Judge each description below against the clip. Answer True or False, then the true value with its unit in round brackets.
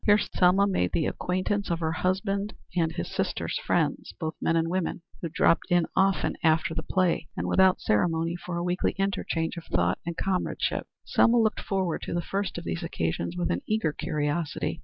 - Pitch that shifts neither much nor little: True (3.0 semitones)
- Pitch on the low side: False (170 Hz)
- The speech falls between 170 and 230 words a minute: True (190 wpm)